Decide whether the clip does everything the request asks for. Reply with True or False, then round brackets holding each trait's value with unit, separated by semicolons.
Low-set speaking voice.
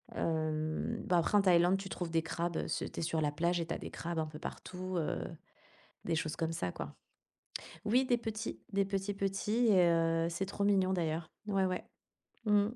False (175 Hz)